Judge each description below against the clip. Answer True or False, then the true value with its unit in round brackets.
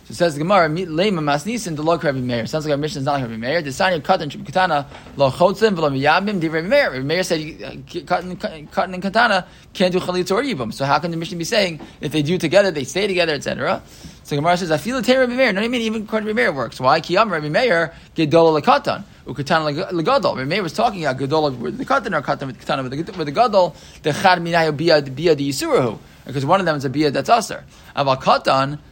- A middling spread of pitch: True (4.0 semitones)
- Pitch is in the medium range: True (165 Hz)